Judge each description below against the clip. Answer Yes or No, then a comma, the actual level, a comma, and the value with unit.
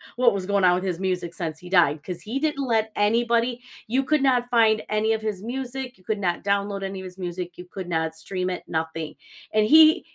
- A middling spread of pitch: Yes, average, 4.7 semitones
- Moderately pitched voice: No, high, 200 Hz